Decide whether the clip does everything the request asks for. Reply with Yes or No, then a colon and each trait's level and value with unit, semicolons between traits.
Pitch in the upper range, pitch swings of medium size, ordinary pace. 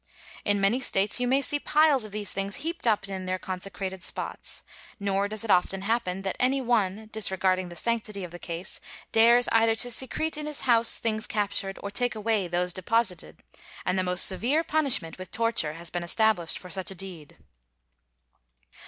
Yes: high, 205 Hz; average, 3.9 semitones; average, 185 wpm